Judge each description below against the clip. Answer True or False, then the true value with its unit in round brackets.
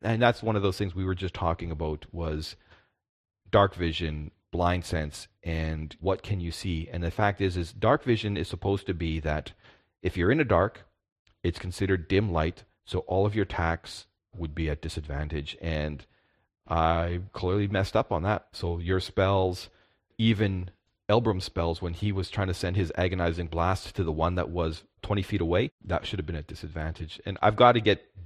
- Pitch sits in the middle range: False (90 Hz)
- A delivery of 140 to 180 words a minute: False (195 wpm)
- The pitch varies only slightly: False (3.3 semitones)